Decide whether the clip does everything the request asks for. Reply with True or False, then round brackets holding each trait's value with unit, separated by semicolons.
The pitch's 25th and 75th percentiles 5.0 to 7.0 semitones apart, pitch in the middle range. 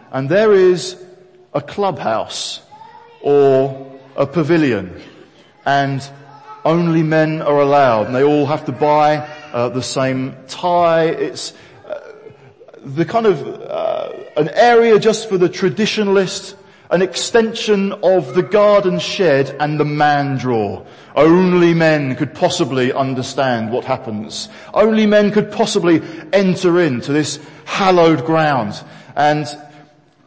True (5.3 semitones; 160 Hz)